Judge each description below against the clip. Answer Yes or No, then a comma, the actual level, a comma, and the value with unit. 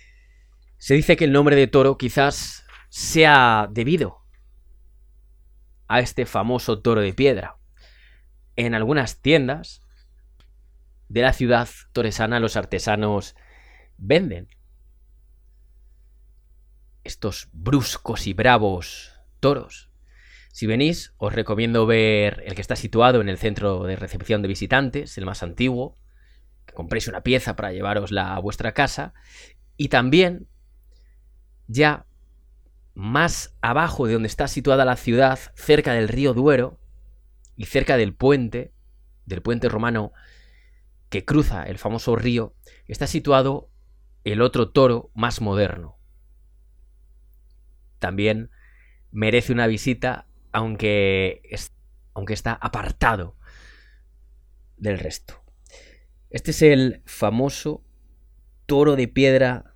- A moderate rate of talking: No, slow, 110 wpm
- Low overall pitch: Yes, low, 105 Hz